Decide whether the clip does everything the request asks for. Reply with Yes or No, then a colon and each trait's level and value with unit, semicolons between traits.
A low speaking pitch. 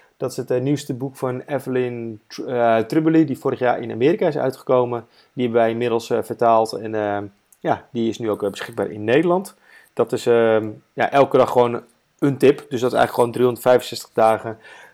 Yes: low, 125 Hz